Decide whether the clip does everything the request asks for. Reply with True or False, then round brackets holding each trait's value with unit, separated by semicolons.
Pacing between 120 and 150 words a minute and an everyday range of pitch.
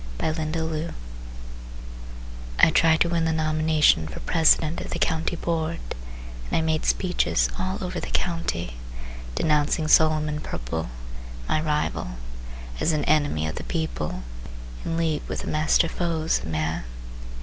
False (140 wpm; 1.6 semitones)